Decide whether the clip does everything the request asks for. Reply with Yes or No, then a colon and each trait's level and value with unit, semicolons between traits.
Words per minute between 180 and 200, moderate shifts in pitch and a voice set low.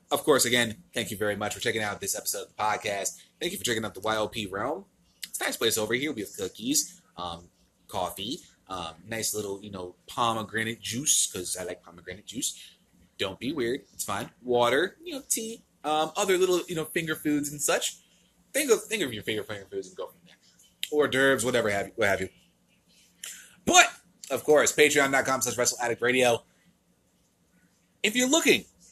No: average, 185 wpm; wide, 8.3 semitones; low, 130 Hz